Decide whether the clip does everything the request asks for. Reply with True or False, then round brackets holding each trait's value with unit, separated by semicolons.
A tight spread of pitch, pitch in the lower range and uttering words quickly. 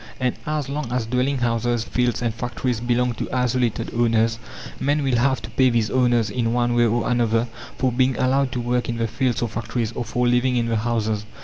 True (1.6 semitones; 120 Hz; 215 wpm)